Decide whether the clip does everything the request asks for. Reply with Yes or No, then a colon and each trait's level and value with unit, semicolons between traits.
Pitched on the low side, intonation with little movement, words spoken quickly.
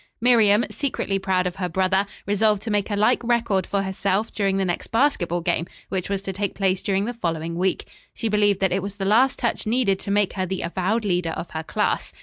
No: high, 195 Hz; narrow, 2.3 semitones; fast, 225 wpm